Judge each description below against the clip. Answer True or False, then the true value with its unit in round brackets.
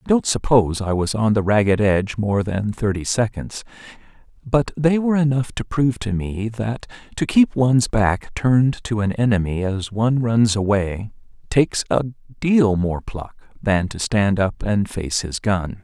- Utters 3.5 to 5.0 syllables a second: True (4.6 syllables/s)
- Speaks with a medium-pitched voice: False (110 Hz)